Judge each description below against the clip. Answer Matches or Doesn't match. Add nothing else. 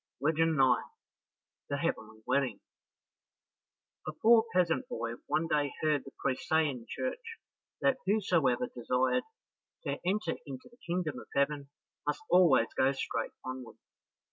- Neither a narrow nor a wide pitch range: Doesn't match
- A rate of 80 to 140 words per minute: Matches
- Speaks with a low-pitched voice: Doesn't match